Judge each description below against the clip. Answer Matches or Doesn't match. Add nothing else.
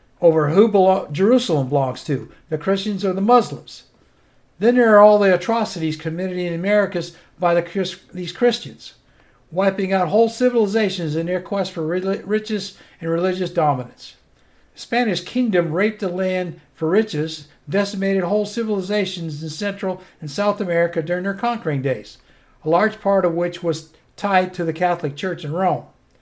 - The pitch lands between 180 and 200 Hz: Matches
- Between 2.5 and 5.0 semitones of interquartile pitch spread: Matches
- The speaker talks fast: Doesn't match